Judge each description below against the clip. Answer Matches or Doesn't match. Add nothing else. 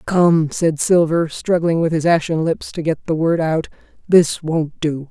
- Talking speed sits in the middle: Matches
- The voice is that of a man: Doesn't match